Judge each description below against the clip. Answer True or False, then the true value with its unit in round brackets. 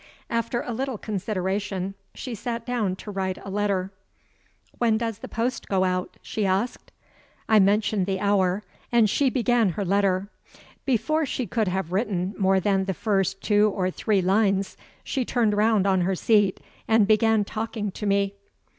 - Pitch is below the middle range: False (205 Hz)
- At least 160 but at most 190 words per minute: True (165 wpm)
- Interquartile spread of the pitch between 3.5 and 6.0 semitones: False (2.7 semitones)